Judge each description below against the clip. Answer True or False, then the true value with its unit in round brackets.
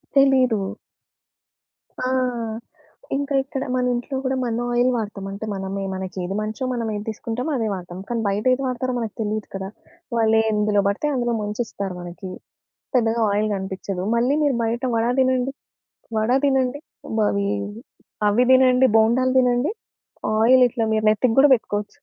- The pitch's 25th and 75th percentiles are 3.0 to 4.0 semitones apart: True (3.6 semitones)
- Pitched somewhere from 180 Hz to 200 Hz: False (225 Hz)